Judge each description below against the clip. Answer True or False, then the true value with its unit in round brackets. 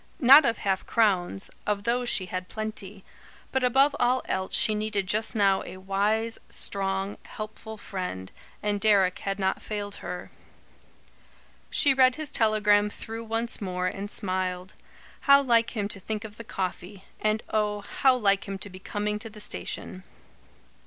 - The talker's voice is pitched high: True (210 Hz)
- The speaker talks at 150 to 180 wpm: True (160 wpm)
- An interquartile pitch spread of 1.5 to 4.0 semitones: True (2.7 semitones)